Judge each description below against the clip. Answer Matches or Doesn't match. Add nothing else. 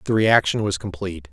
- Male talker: Matches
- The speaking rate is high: Doesn't match